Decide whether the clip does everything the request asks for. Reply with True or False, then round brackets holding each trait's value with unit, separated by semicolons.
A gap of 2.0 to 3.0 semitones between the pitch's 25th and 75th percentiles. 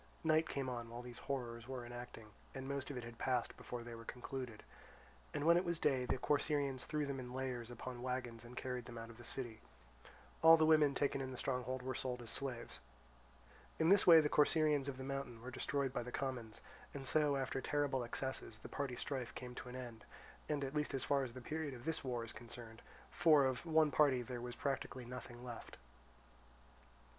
True (2.7 semitones)